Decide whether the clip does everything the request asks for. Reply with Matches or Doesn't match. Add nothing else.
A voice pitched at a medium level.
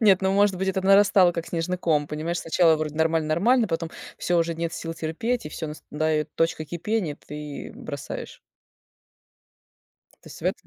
Matches